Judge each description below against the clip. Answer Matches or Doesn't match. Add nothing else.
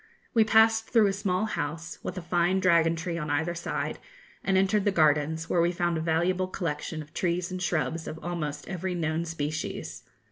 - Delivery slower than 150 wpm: Doesn't match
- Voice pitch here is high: Doesn't match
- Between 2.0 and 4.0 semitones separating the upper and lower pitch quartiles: Matches